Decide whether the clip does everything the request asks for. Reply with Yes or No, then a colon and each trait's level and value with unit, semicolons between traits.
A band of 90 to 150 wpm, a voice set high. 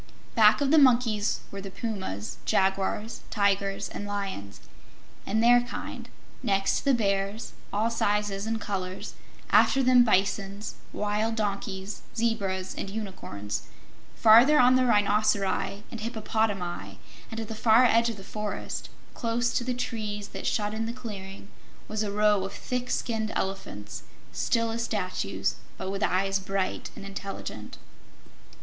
Yes: average, 145 wpm; high, 210 Hz